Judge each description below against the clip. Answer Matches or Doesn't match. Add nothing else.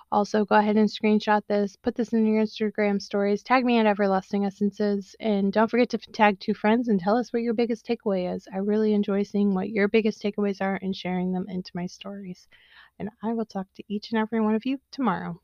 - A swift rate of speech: Matches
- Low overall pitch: Doesn't match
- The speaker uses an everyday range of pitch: Doesn't match